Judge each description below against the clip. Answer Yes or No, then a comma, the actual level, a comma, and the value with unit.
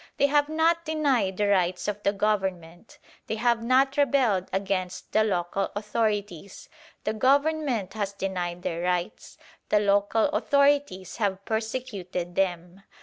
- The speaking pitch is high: Yes, high, 205 Hz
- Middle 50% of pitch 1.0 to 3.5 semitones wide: No, wide, 5.5 semitones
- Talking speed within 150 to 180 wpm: No, slow, 135 wpm